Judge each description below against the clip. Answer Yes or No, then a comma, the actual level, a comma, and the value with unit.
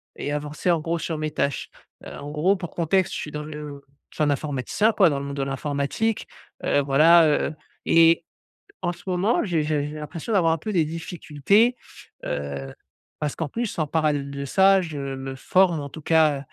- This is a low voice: No, medium, 155 Hz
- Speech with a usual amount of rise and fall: Yes, average, 3.3 semitones